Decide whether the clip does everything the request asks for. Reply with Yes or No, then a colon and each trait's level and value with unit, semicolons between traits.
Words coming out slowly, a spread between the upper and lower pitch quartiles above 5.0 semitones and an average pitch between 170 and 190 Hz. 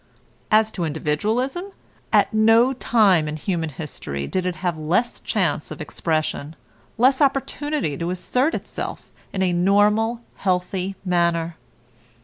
Yes: slow, 130 wpm; wide, 5.6 semitones; medium, 185 Hz